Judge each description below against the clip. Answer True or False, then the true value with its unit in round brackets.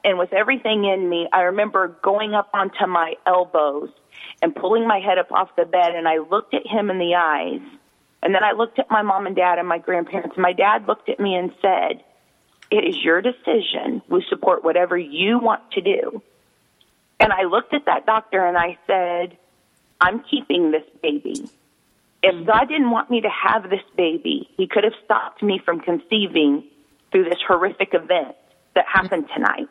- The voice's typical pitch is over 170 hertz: True (190 Hz)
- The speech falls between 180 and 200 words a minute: True (190 wpm)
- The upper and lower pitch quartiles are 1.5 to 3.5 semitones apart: False (4.4 semitones)